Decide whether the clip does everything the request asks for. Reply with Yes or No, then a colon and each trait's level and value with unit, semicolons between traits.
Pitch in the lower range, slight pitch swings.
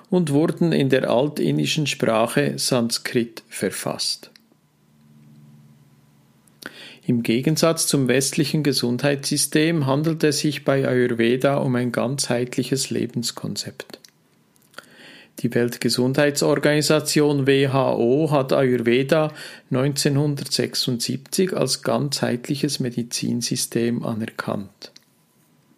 No: low, 130 Hz; average, 3.7 semitones